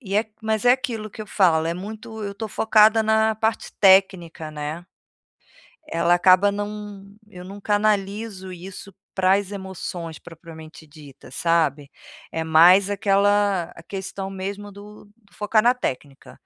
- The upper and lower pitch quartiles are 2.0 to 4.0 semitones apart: Yes, average, 3.6 semitones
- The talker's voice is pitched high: Yes, high, 195 Hz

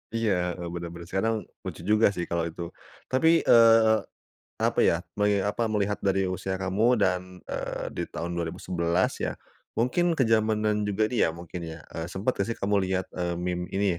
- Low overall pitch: Yes, very low, 95 Hz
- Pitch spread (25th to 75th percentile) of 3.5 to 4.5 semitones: Yes, average, 3.9 semitones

